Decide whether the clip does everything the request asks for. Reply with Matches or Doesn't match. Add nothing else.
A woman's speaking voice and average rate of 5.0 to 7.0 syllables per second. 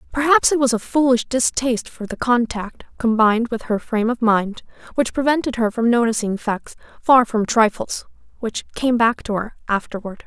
Matches